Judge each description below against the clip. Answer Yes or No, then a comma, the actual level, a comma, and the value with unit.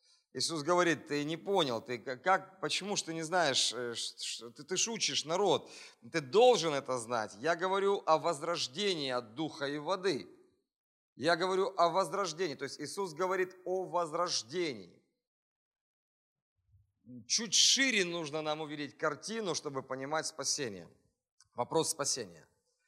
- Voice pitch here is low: No, medium, 165 Hz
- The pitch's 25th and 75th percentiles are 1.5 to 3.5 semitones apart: No, wide, 5.4 semitones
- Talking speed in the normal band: Yes, average, 130 wpm